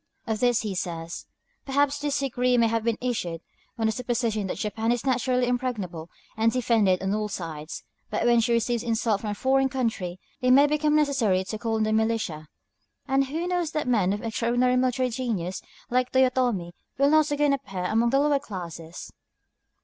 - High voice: Yes, high, 235 Hz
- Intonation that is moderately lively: Yes, average, 3.9 semitones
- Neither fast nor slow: Yes, average, 185 wpm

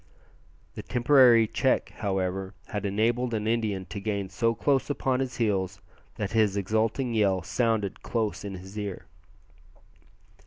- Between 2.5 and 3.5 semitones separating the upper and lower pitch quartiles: Yes, average, 3.1 semitones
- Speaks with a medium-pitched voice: No, low, 105 Hz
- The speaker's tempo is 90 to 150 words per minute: Yes, average, 140 wpm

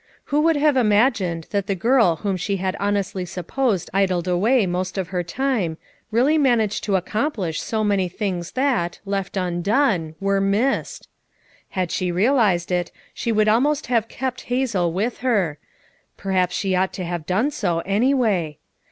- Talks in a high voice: Yes, high, 200 Hz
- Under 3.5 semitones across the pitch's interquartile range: No, average, 5.0 semitones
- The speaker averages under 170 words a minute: Yes, average, 160 wpm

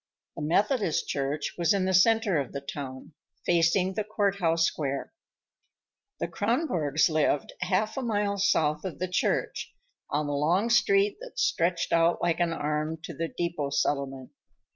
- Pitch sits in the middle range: Yes, medium, 170 Hz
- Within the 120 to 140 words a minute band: No, average, 160 wpm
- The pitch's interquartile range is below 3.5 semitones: No, average, 5.1 semitones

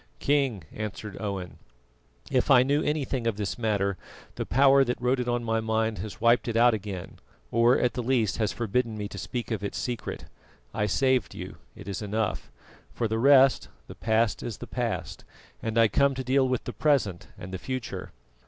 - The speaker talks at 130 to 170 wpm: No, average, 195 wpm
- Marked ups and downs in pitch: No, average, 3.3 semitones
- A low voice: Yes, low, 115 Hz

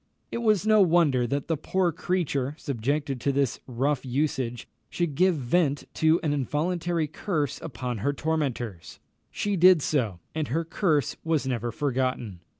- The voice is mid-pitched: Yes, medium, 145 Hz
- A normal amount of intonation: Yes, average, 4.5 semitones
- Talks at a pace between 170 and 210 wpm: No, average, 150 wpm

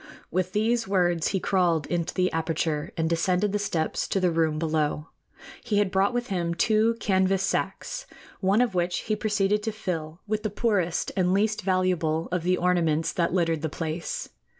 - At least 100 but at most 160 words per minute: No, average, 180 wpm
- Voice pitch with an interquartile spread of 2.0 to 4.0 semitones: Yes, average, 3.7 semitones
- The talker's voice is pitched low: No, medium, 180 Hz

